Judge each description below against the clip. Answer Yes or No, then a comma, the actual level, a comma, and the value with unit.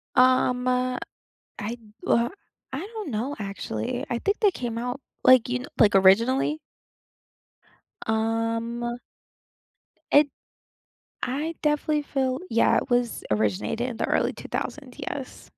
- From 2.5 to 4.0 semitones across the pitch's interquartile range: Yes, average, 2.8 semitones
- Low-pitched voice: No, high, 245 Hz